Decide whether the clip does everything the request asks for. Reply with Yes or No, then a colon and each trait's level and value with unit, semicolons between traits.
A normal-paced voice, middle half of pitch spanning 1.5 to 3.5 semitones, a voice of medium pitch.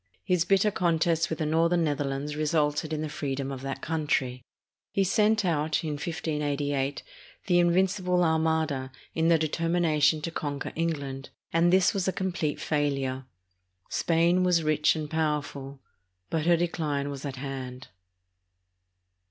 Yes: average, 145 wpm; average, 3.0 semitones; medium, 155 Hz